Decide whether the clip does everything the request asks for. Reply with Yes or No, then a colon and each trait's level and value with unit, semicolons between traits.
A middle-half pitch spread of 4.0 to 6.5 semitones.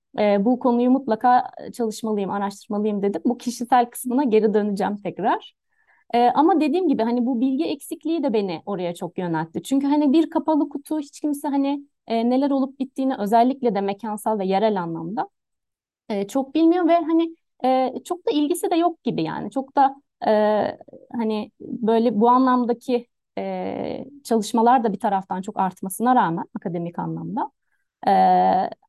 Yes: wide, 5.4 semitones